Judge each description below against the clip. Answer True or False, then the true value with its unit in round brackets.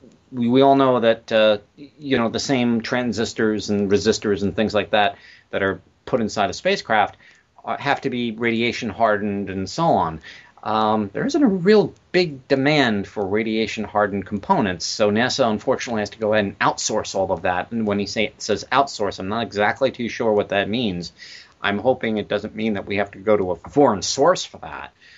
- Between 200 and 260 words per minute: True (205 wpm)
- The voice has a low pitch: True (110 Hz)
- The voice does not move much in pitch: False (3.6 semitones)